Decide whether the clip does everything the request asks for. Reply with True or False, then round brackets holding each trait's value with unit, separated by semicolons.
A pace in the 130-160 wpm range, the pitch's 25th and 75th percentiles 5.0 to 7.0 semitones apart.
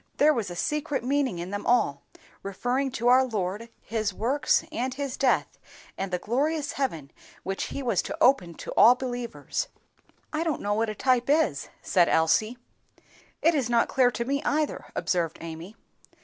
False (175 wpm; 5.6 semitones)